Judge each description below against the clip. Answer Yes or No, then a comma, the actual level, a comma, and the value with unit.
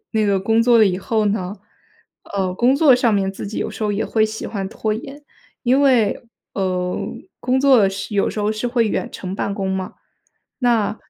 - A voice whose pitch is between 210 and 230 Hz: Yes, high, 215 Hz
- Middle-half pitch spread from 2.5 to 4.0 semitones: Yes, average, 3.4 semitones